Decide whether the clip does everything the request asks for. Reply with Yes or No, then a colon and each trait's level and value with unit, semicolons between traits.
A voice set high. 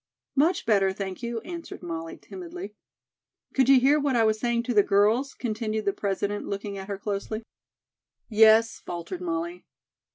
Yes: high, 220 Hz